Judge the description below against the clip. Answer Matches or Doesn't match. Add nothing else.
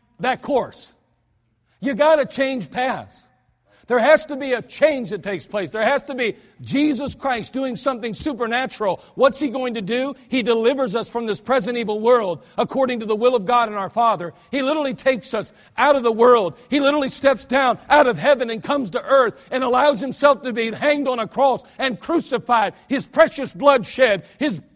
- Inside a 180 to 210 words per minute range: Matches